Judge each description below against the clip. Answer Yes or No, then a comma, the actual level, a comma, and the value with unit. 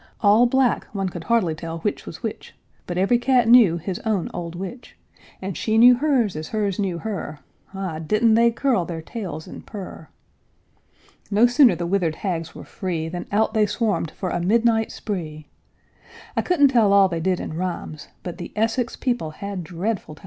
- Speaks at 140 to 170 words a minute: No, average, 185 wpm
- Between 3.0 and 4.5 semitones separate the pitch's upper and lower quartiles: No, average, 5.1 semitones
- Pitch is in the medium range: No, high, 200 Hz